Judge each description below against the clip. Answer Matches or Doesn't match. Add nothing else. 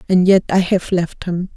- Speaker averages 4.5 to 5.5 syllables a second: Matches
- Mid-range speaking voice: Matches